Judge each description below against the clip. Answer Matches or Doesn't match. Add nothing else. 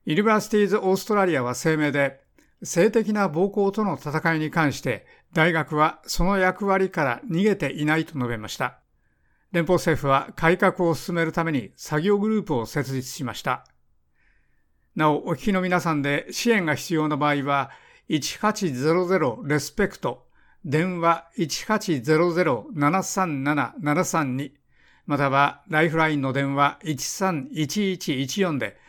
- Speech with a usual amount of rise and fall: Matches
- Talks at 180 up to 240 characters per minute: Doesn't match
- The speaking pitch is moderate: Matches